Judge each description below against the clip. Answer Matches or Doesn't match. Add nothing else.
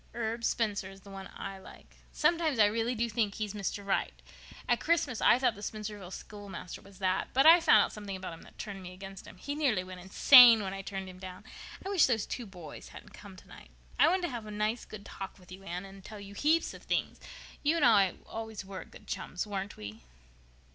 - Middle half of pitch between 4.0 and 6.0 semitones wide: Doesn't match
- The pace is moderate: Doesn't match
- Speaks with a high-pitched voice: Matches